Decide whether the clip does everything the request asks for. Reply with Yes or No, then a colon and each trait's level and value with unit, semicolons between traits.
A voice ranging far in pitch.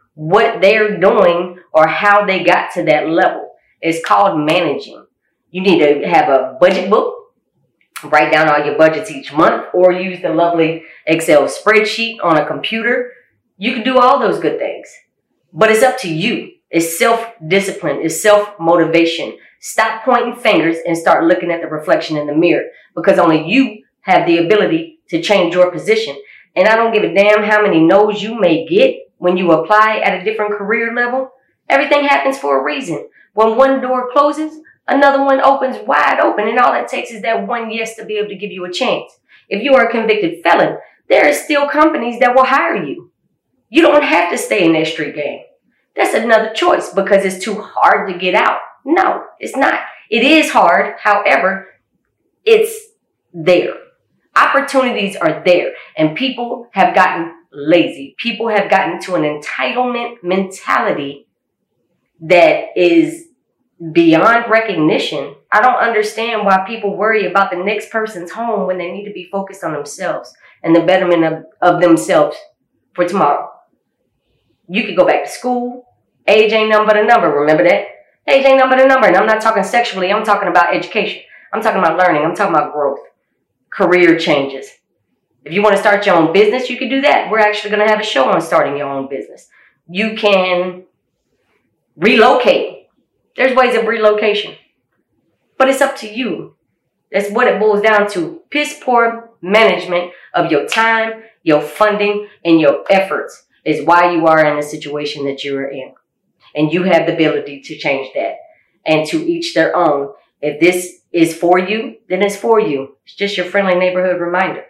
Yes: wide, 5.9 semitones